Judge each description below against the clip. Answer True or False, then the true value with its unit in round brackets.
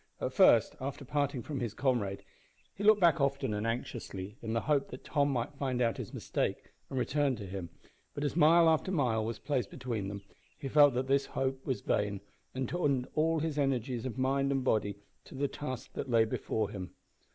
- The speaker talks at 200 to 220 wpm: True (205 wpm)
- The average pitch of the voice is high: False (130 Hz)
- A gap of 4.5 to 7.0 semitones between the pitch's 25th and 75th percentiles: False (3.8 semitones)